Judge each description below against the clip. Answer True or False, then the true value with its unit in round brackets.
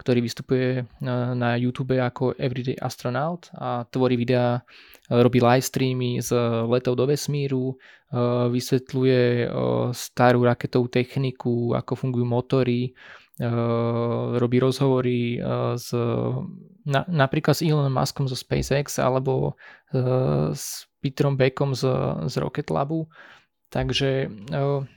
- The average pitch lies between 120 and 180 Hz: True (125 Hz)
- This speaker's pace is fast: False (105 wpm)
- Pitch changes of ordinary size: False (1.7 semitones)